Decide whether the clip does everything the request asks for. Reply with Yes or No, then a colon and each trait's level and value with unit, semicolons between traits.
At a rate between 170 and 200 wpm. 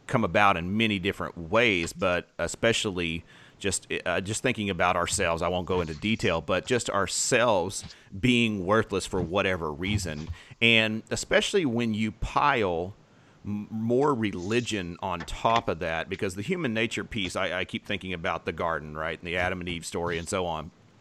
Yes: average, 175 wpm